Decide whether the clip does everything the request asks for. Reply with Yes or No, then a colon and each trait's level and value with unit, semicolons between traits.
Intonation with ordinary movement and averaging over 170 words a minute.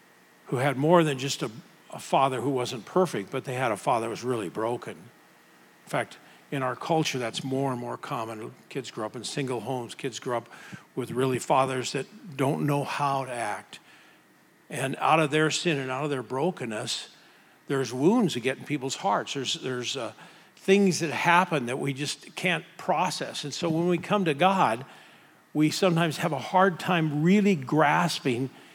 Yes: average, 4.5 semitones; average, 190 wpm